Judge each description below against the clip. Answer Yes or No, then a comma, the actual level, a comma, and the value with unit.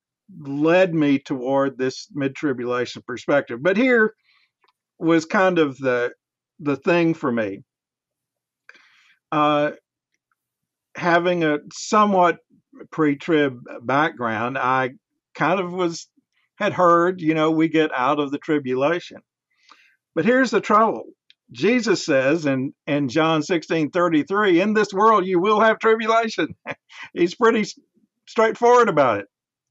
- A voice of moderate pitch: Yes, medium, 165 Hz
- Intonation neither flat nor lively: No, wide, 6.8 semitones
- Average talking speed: No, slow, 120 wpm